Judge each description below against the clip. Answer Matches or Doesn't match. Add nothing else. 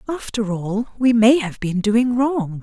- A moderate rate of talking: Matches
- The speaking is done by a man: Doesn't match